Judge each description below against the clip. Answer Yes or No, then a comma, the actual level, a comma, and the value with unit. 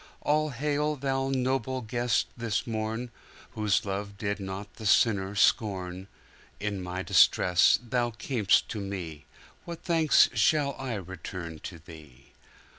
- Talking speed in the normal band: No, slow, 115 wpm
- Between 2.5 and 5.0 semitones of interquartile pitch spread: No, wide, 5.4 semitones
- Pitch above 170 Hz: No, low, 110 Hz